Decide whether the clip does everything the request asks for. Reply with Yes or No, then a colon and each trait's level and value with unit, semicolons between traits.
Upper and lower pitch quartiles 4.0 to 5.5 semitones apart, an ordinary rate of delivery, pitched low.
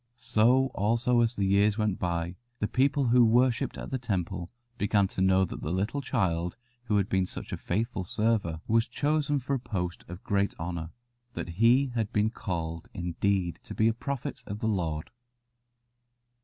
Yes: average, 4.9 semitones; average, 180 wpm; low, 105 Hz